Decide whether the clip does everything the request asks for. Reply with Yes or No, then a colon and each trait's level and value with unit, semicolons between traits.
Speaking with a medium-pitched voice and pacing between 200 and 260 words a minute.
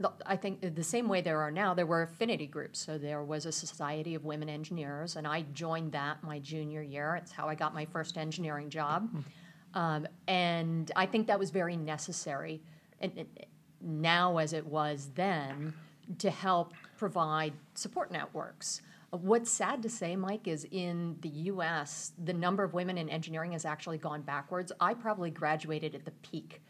No: medium, 165 Hz; average, 180 wpm